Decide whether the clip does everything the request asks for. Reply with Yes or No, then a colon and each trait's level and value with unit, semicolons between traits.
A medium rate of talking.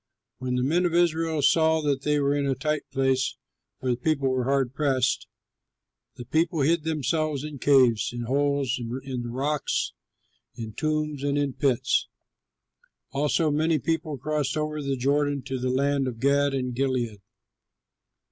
Yes: average, 160 wpm